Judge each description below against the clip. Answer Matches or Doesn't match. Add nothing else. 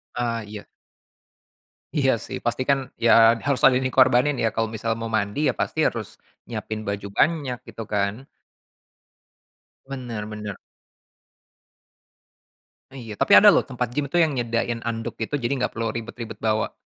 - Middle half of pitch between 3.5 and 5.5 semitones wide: Doesn't match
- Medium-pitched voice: Doesn't match